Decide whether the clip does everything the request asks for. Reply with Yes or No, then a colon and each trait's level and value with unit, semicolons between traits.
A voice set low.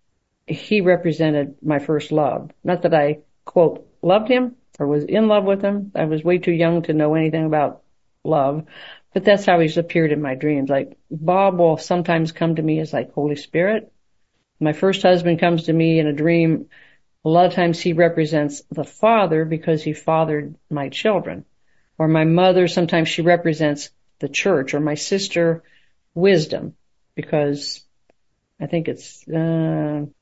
No: medium, 160 Hz